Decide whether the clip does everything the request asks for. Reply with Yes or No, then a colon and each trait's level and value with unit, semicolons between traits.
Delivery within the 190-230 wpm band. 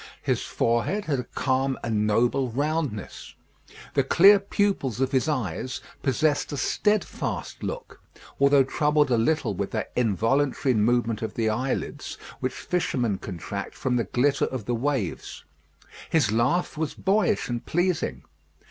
No: average, 140 wpm